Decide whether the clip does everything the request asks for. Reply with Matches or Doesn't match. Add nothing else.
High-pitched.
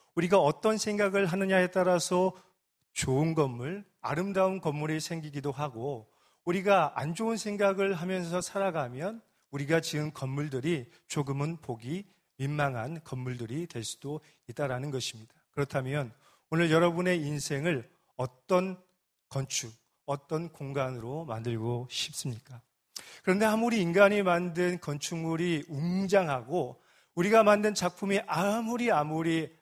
Doesn't match